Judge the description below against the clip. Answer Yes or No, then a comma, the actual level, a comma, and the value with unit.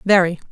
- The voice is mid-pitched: Yes, medium, 180 Hz